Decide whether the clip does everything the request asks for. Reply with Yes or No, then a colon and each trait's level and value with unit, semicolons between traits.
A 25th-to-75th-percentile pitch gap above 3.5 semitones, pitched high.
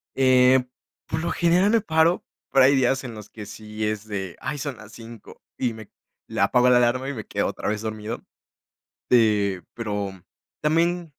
No: average, 4.7 semitones; low, 120 Hz